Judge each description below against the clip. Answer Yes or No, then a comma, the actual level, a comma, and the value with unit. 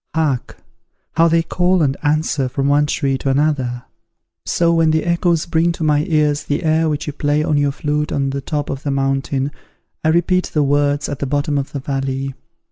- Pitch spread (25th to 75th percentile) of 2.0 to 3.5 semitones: Yes, narrow, 2.4 semitones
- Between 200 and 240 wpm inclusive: Yes, fast, 205 wpm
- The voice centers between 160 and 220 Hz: No, medium, 145 Hz